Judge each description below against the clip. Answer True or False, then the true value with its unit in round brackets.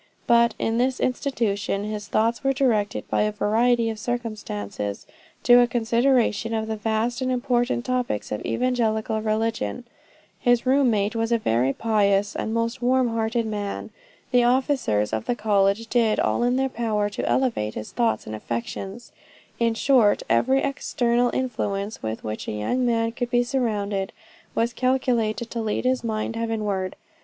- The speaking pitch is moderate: False (230 Hz)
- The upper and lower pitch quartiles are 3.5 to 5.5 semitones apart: False (2.7 semitones)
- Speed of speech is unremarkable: True (160 wpm)